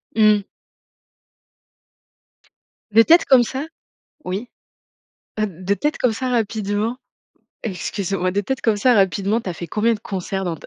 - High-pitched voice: Yes, high, 210 Hz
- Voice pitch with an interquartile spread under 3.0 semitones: No, average, 3.3 semitones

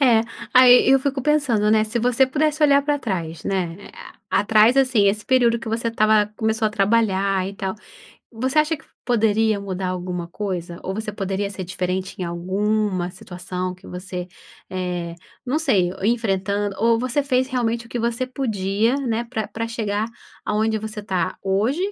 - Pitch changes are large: No, average, 4.1 semitones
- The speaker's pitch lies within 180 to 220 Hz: Yes, high, 215 Hz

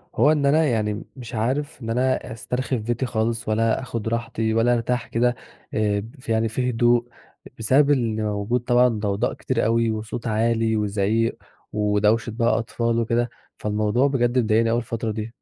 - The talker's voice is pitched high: No, low, 115 Hz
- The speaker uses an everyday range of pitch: No, narrow, 1.9 semitones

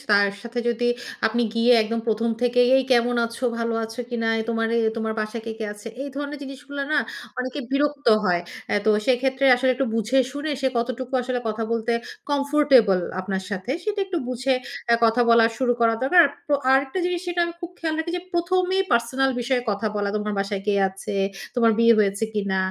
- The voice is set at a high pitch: Yes, high, 245 Hz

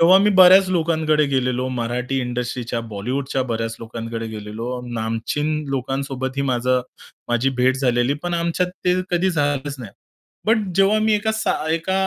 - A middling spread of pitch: No, wide, 5.7 semitones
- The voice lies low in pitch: Yes, low, 130 Hz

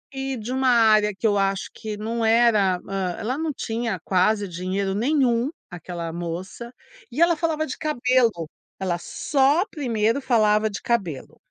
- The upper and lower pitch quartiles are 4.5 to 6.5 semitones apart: Yes, average, 4.9 semitones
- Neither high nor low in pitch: No, high, 220 Hz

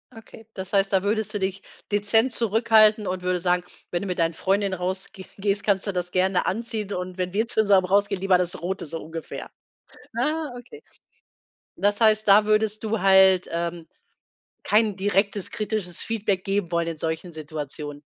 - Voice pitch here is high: Yes, high, 195 Hz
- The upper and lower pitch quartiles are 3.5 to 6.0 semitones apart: No, average, 2.8 semitones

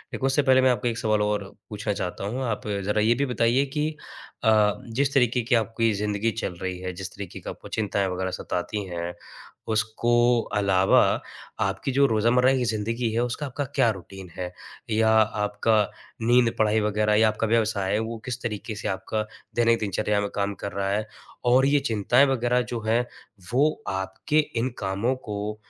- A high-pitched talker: No, low, 110 Hz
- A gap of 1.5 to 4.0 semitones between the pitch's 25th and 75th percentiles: Yes, average, 2.9 semitones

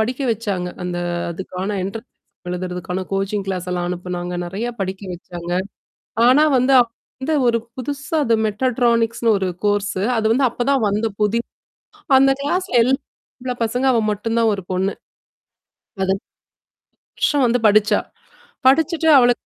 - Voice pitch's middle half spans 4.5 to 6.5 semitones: Yes, average, 4.9 semitones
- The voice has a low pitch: No, high, 220 Hz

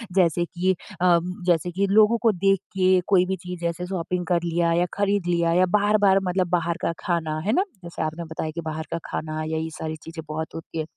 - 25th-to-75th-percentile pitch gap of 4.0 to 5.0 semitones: No, narrow, 2.5 semitones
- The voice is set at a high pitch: No, medium, 175 Hz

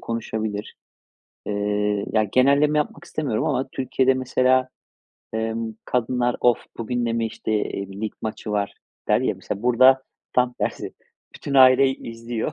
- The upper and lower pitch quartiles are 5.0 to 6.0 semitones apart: No, average, 2.9 semitones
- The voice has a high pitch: No, low, 120 Hz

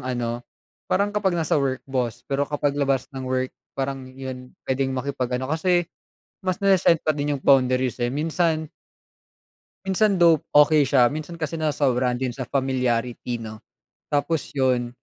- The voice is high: No, low, 135 Hz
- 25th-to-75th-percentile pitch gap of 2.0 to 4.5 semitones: Yes, average, 3.6 semitones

